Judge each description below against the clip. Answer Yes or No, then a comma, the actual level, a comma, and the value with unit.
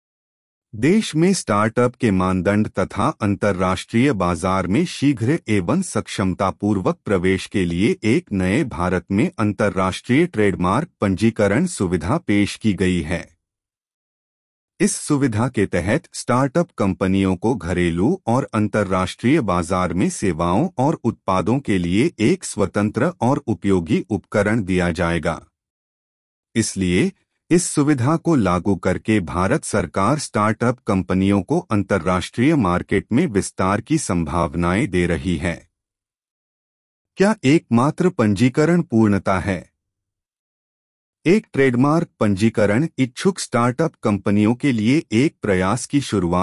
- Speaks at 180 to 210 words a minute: No, average, 115 wpm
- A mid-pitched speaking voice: No, low, 105 Hz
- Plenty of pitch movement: No, average, 5.0 semitones